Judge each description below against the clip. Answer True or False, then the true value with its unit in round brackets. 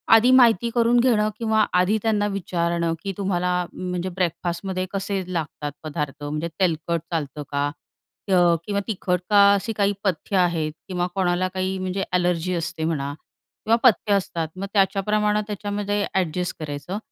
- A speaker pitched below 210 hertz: True (185 Hz)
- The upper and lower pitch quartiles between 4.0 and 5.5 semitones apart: False (3.2 semitones)